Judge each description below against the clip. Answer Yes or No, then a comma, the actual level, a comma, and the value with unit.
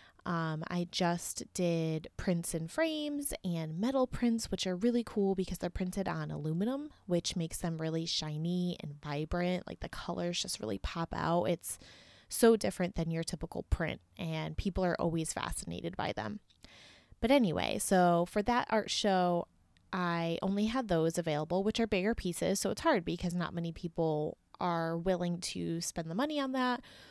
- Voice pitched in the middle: Yes, medium, 175 Hz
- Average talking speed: Yes, average, 175 wpm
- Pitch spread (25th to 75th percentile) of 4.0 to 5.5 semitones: No, average, 3.4 semitones